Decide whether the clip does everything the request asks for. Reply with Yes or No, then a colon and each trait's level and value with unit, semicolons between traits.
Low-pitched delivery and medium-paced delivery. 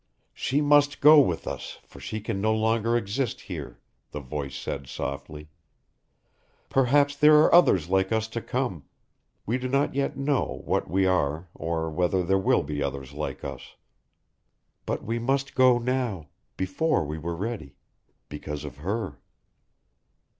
Yes: very low, 95 Hz; average, 155 wpm